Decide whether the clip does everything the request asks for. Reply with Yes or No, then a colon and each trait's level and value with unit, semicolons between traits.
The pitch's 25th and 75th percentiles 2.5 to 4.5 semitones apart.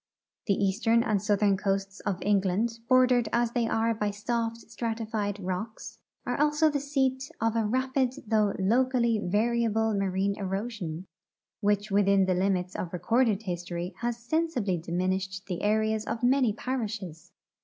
Yes: average, 3.3 semitones